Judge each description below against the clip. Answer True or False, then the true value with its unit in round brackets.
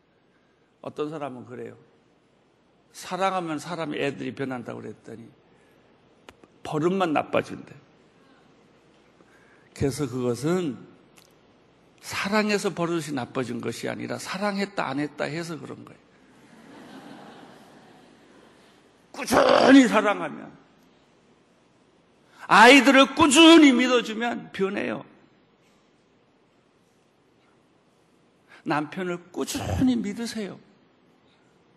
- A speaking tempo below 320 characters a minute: True (185 characters per minute)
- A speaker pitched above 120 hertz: True (185 Hz)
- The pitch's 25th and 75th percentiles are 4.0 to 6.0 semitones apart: False (8.5 semitones)